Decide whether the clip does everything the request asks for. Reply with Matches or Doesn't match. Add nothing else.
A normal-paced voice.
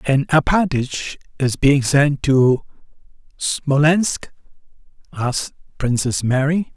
Doesn't match